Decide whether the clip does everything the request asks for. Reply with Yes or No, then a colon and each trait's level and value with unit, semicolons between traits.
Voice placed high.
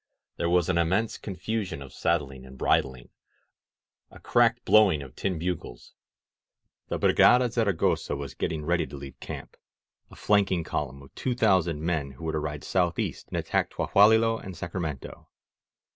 No: very low, 85 Hz